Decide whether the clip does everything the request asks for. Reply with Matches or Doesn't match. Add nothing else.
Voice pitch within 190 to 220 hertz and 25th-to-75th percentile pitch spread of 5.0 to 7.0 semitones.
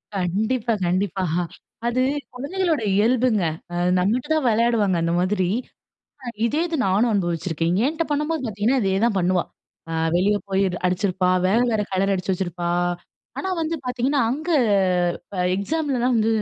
Matches